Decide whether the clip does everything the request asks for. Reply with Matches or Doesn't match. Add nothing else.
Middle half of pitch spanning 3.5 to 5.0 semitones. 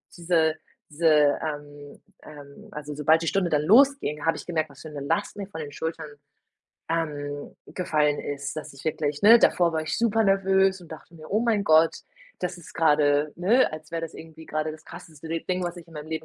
Doesn't match